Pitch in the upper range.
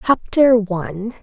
Yes: high, 215 Hz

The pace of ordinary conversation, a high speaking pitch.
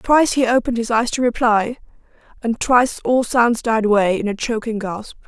Yes: average, 195 wpm; high, 230 Hz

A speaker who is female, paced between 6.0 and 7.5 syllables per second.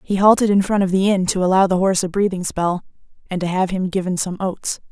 Yes: female; 6.1 syllables/s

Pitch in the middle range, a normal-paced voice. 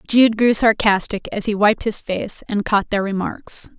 No: high, 210 Hz; average, 190 wpm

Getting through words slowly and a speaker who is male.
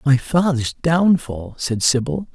Yes: slow, 130 wpm; male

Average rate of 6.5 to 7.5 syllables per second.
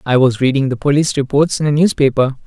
Yes: 6.6 syllables/s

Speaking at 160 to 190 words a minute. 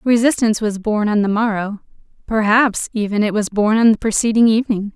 Yes: average, 180 wpm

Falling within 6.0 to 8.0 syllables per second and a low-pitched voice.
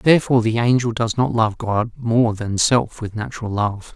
No: 4.9 syllables/s; low, 115 Hz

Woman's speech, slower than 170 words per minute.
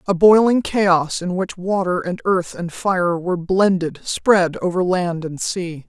No: female; average, 175 wpm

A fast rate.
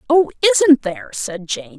No: average, 170 wpm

